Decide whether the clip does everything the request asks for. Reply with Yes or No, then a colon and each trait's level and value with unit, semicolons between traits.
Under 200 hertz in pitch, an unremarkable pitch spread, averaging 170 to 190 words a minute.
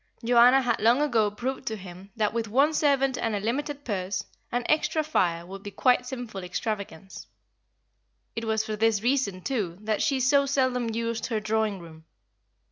No: high, 225 Hz; average, 4.2 semitones; average, 180 wpm